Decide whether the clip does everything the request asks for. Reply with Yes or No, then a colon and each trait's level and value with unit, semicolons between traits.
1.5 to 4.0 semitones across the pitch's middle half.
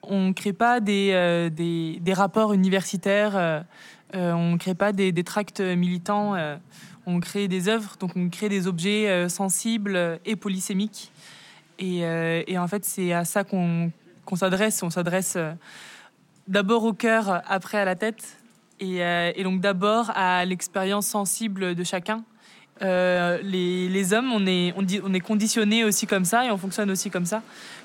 Yes: narrow, 2.6 semitones